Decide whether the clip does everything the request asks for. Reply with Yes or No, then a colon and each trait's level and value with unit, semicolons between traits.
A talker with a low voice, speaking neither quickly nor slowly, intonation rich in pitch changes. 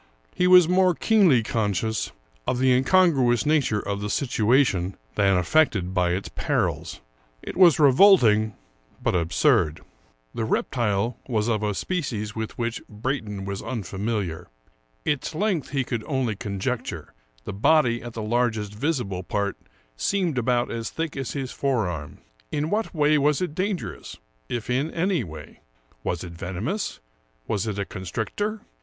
Yes: low, 120 Hz; average, 150 wpm; wide, 6.5 semitones